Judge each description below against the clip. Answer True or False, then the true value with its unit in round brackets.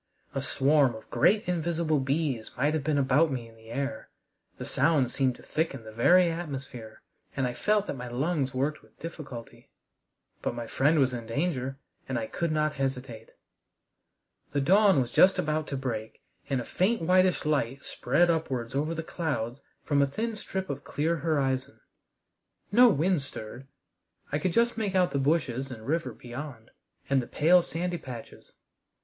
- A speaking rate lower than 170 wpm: False (175 wpm)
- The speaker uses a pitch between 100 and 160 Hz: True (140 Hz)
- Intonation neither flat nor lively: True (4.6 semitones)